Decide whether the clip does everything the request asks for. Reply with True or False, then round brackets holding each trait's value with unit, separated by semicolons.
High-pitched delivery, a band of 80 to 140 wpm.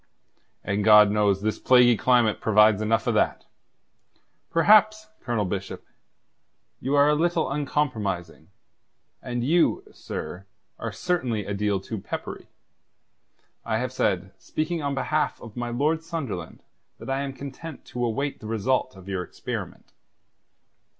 False (120 Hz; 135 wpm)